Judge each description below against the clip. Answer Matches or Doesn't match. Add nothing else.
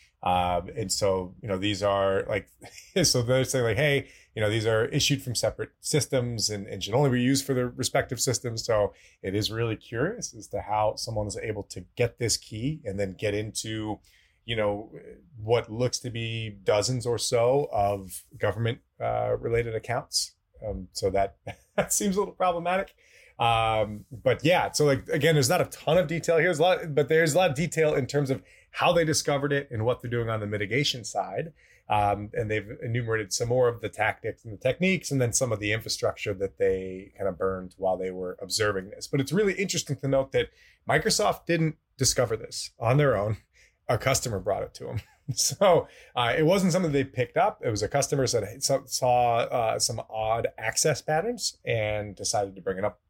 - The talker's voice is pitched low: Matches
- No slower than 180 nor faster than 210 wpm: Matches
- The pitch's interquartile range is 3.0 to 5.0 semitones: Doesn't match